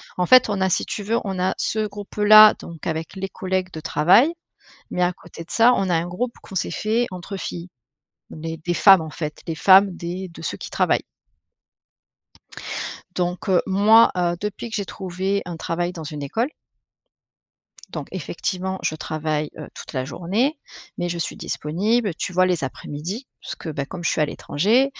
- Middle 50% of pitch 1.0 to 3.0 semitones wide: No, average, 3.6 semitones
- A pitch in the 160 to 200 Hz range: Yes, medium, 185 Hz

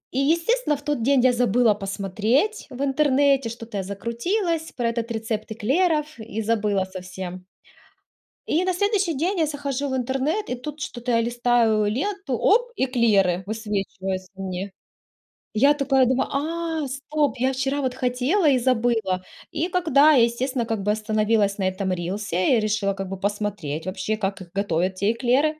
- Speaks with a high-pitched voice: Yes, high, 240 Hz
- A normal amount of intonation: No, wide, 5.8 semitones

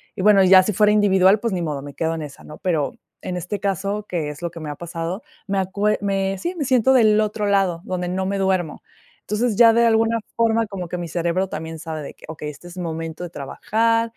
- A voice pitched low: No, high, 190 Hz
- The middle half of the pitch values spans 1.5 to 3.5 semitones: No, average, 4.1 semitones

